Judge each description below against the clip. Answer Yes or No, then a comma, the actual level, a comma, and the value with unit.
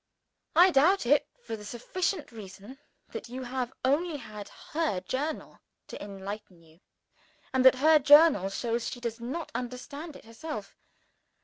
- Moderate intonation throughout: No, wide, 5.8 semitones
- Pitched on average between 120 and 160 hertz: No, very high, 255 Hz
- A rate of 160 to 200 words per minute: No, average, 145 wpm